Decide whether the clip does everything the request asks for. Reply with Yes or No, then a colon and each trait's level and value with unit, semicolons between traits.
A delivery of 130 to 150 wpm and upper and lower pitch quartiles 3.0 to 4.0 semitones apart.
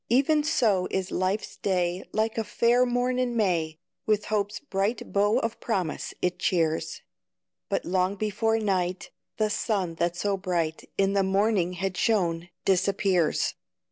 Yes: average, 145 wpm; average, 3.4 semitones